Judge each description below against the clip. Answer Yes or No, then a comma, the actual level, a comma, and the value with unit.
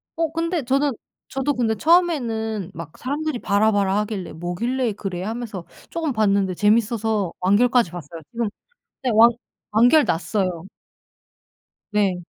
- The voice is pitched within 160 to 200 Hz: No, high, 220 Hz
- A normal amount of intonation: Yes, average, 4.7 semitones